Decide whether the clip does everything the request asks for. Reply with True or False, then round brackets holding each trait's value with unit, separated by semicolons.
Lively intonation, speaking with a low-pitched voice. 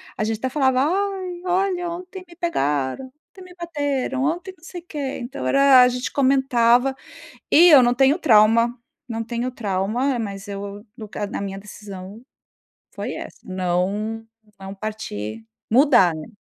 False (6.4 semitones; 250 Hz)